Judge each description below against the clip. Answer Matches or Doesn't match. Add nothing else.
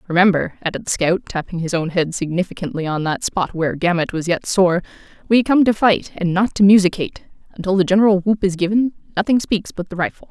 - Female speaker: Matches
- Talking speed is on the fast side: Matches